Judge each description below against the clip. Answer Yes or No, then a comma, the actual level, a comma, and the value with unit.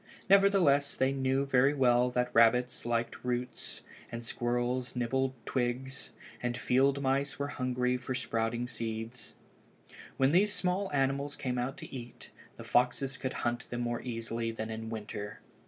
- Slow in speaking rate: No, average, 155 wpm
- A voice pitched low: Yes, low, 125 Hz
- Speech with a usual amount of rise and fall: No, narrow, 2.2 semitones